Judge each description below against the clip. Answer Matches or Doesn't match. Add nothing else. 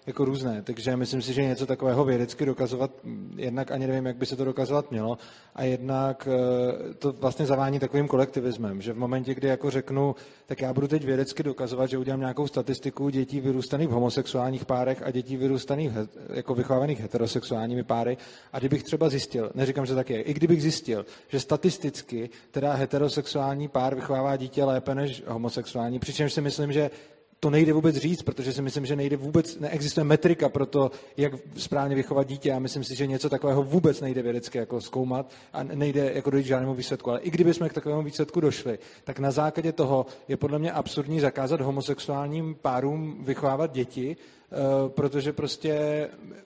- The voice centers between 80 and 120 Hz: Doesn't match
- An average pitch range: Doesn't match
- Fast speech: Matches